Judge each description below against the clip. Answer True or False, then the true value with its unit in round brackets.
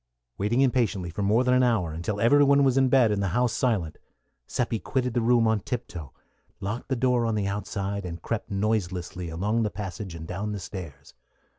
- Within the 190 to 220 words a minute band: True (200 wpm)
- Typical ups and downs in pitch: True (4.7 semitones)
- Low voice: True (105 Hz)